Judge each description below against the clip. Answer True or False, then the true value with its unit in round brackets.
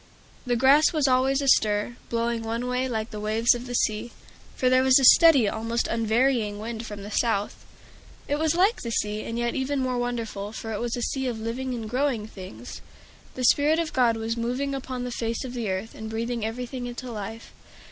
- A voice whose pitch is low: False (235 Hz)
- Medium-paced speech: False (210 wpm)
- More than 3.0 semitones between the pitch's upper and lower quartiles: False (2.6 semitones)